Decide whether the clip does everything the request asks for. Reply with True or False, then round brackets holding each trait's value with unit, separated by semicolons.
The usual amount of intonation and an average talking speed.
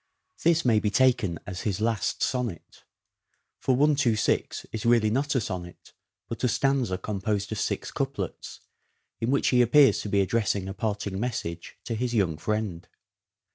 True (4.0 semitones; 160 wpm)